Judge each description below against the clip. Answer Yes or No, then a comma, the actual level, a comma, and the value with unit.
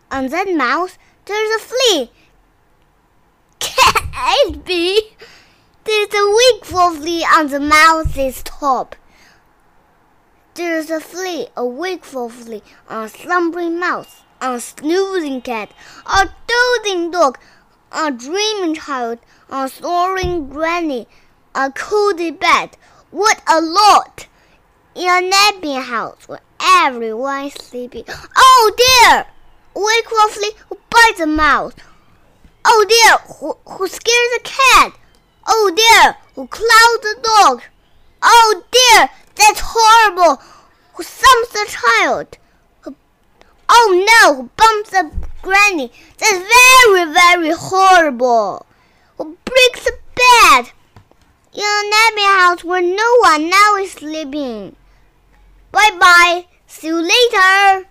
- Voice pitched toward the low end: No, very high, 375 Hz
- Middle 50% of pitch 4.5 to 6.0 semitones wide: Yes, average, 5.3 semitones